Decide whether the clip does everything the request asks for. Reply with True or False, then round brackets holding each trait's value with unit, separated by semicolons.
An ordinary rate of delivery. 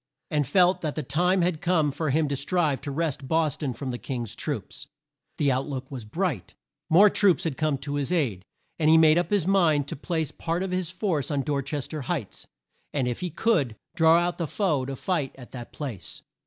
False (220 wpm)